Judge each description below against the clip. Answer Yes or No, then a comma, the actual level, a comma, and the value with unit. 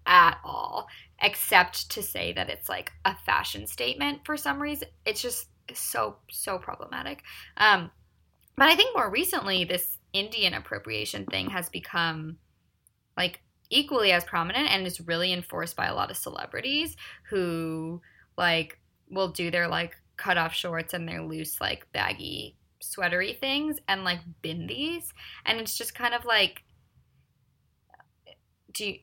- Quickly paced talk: No, average, 145 wpm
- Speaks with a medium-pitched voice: Yes, medium, 180 Hz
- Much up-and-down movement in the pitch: Yes, wide, 6.2 semitones